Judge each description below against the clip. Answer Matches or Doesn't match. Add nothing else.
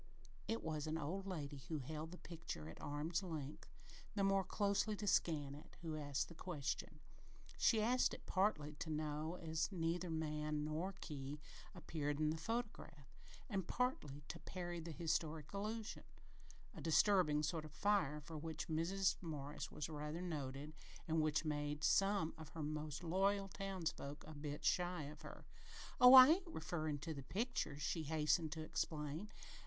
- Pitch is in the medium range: Matches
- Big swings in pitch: Doesn't match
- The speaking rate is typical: Matches